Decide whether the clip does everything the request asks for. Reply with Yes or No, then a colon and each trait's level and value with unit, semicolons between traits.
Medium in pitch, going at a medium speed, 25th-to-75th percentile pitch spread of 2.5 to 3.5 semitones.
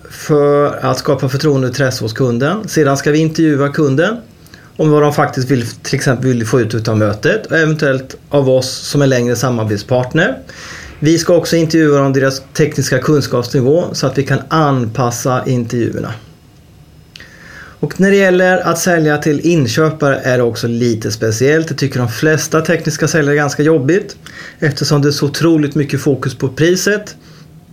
Yes: medium, 145 Hz; average, 170 wpm; average, 3.2 semitones